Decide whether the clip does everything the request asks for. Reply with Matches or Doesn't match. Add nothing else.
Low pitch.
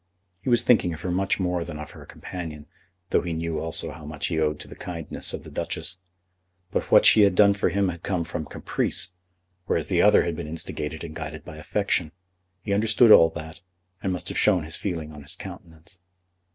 Matches